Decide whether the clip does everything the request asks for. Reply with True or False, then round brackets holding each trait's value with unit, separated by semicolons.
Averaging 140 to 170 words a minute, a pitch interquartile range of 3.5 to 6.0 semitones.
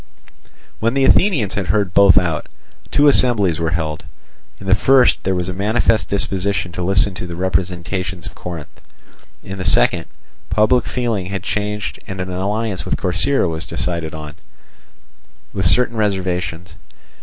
False (155 wpm; 3.1 semitones)